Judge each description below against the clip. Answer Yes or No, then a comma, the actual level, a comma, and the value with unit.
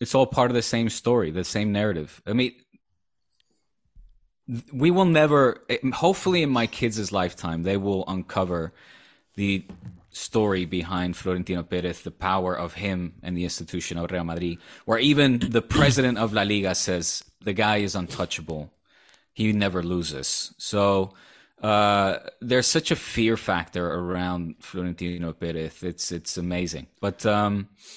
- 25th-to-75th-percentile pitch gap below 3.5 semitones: No, average, 4.4 semitones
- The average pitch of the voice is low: Yes, very low, 95 Hz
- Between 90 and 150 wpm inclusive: Yes, average, 145 wpm